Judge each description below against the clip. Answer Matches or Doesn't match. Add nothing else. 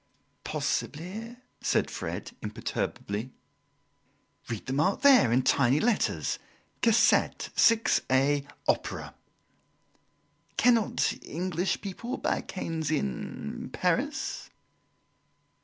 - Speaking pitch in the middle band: Matches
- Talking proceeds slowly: Matches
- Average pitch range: Doesn't match